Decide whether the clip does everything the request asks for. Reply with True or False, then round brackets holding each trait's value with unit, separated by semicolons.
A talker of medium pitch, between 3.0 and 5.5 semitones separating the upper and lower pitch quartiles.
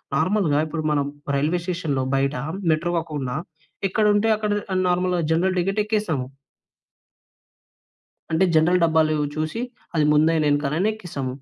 True (160 Hz; 3.7 semitones)